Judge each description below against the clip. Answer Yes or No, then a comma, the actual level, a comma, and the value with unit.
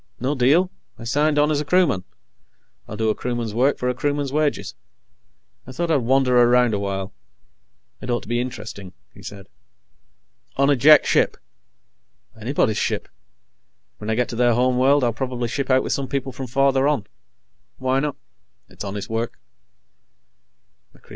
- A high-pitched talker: No, low, 125 Hz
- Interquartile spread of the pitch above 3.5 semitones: No, average, 3.2 semitones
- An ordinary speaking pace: Yes, average, 165 wpm